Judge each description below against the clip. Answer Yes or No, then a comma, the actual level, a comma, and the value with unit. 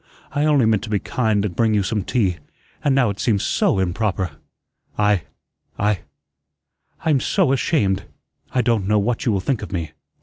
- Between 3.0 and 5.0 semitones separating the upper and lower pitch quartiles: Yes, average, 3.8 semitones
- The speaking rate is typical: Yes, average, 180 wpm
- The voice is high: No, low, 105 Hz